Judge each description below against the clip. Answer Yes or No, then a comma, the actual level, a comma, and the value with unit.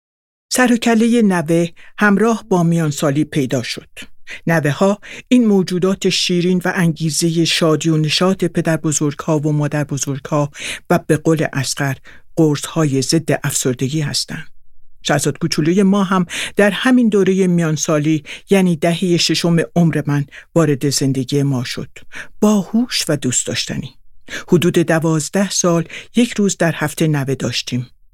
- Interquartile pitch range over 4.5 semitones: No, average, 4.0 semitones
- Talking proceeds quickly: No, average, 140 wpm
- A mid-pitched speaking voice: Yes, medium, 165 Hz